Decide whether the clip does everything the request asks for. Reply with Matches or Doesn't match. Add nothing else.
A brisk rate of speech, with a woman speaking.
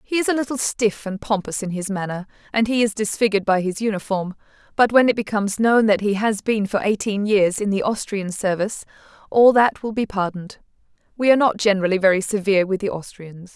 Matches